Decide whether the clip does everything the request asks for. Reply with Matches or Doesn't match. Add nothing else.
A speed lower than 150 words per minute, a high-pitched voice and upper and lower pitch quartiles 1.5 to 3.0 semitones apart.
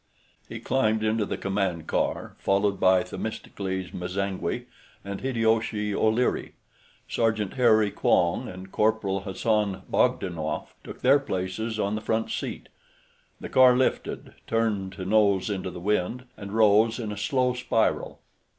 Doesn't match